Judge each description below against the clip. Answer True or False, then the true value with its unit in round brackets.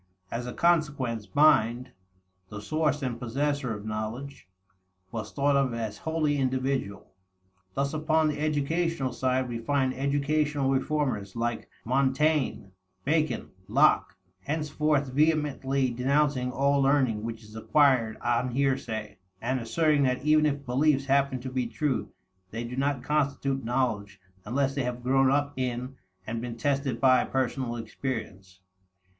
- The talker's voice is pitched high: False (135 Hz)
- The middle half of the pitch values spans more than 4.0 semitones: False (3.3 semitones)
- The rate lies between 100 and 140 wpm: True (135 wpm)